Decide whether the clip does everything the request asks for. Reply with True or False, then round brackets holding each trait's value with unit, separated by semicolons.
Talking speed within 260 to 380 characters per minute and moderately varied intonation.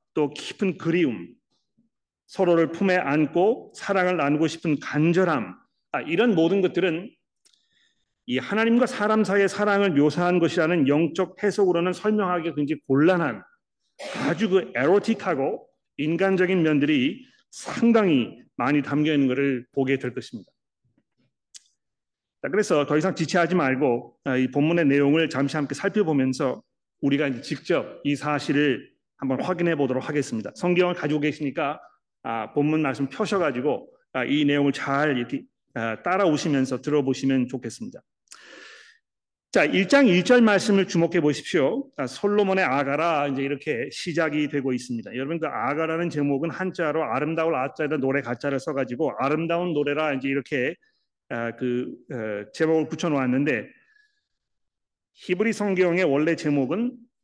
True (310 characters per minute; 5.0 semitones)